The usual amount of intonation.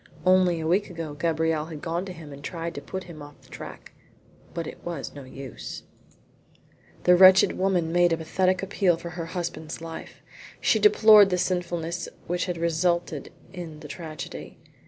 No: narrow, 2.1 semitones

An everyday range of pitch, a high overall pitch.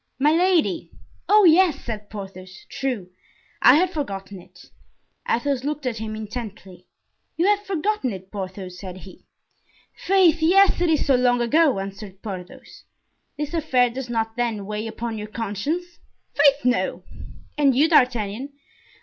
No: wide, 7.1 semitones; high, 245 Hz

